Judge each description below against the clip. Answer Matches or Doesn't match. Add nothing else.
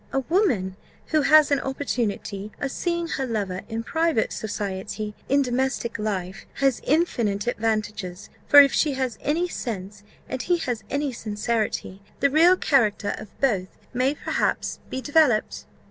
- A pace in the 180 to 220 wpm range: Doesn't match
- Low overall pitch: Doesn't match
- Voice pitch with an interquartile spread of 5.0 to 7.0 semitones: Matches